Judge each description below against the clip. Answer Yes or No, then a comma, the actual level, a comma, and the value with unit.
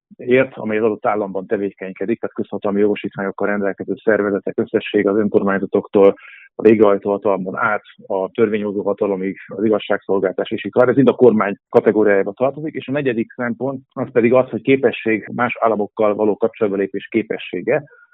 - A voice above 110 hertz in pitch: No, low, 105 Hz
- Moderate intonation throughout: Yes, average, 3.4 semitones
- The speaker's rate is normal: Yes, average, 140 wpm